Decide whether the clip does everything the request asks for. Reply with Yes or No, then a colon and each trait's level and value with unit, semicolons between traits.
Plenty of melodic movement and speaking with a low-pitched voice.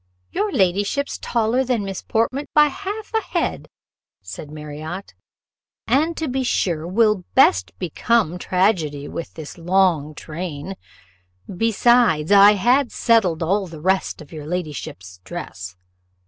No: wide, 6.8 semitones; high, 190 Hz